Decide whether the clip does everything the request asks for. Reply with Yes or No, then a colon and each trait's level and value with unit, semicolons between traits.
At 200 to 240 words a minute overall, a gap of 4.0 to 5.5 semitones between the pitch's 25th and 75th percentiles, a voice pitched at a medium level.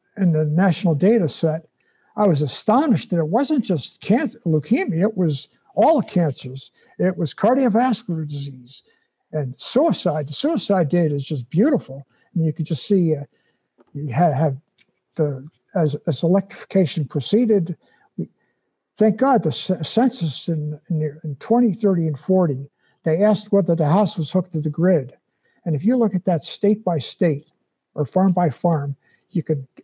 No: average, 165 wpm; average, 4.8 semitones; medium, 170 Hz